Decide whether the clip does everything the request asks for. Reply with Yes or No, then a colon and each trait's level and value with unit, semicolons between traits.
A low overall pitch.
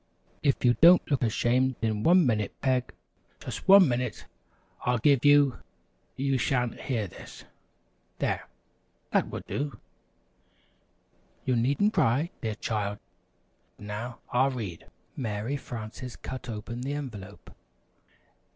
Yes: low, 125 Hz